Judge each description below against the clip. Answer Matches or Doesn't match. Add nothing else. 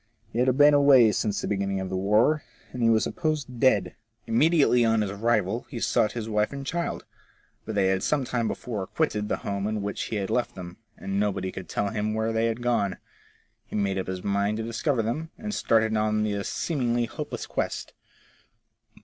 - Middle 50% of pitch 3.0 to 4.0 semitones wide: Matches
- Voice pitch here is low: Matches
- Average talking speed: Doesn't match